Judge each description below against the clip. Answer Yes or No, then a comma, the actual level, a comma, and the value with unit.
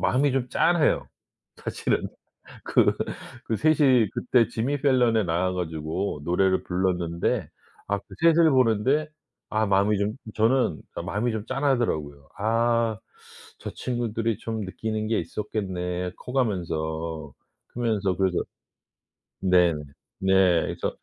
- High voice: No, low, 105 Hz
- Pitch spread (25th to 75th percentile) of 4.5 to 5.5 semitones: Yes, average, 5.2 semitones